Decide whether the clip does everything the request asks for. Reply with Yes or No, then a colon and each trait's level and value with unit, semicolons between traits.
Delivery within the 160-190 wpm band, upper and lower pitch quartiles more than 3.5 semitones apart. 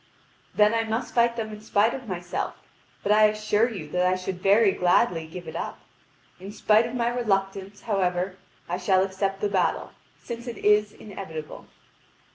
No: average, 175 wpm; average, 3.1 semitones